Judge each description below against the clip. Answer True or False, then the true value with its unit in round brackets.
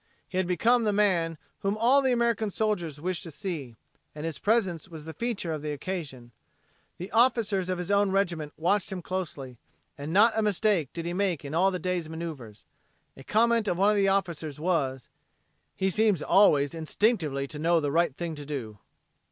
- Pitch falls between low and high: True (175 Hz)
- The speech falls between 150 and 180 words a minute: False (195 wpm)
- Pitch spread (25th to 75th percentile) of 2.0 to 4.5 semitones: False (4.9 semitones)